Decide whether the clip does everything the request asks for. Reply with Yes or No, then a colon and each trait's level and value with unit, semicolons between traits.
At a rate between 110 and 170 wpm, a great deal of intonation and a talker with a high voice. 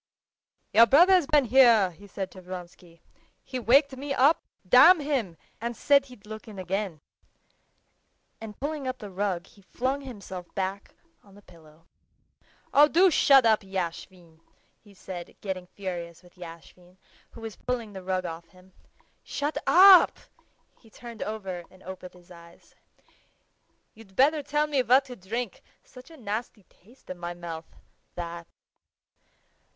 Yes: average, 150 wpm; wide, 6.1 semitones; high, 205 Hz